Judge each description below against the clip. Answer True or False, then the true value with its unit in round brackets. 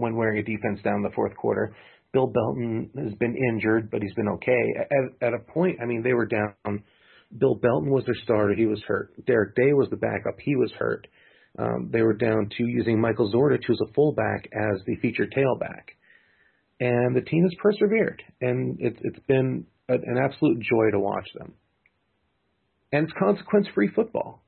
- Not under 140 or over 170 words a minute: False (195 wpm)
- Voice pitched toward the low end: True (120 Hz)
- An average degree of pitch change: True (3.7 semitones)